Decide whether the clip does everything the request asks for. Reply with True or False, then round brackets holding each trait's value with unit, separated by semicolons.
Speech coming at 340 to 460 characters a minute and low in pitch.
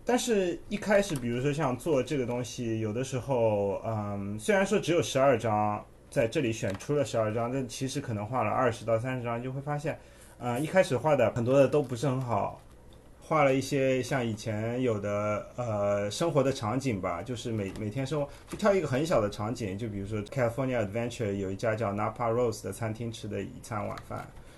True (350 characters per minute; 120 Hz)